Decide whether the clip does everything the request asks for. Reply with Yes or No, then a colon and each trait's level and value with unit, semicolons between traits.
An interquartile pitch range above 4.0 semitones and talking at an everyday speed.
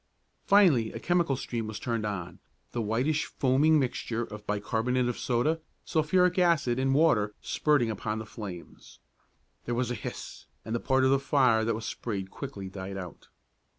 Yes: average, 4.5 semitones; average, 170 wpm